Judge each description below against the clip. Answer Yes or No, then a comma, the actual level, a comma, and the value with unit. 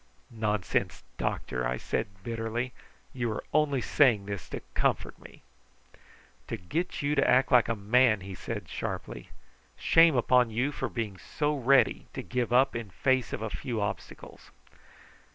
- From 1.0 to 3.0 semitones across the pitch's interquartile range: No, average, 4.0 semitones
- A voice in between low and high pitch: No, low, 120 Hz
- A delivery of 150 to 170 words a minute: Yes, average, 155 wpm